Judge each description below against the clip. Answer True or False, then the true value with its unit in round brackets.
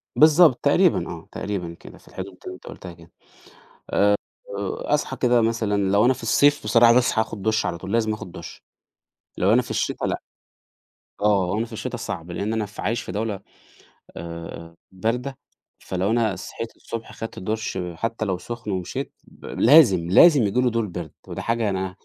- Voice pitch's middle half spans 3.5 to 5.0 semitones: True (3.8 semitones)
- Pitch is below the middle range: True (110 Hz)